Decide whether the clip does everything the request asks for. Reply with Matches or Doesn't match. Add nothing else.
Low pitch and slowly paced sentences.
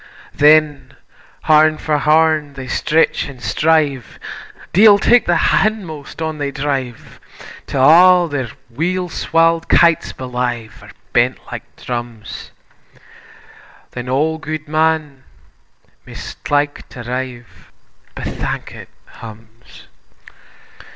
Doesn't match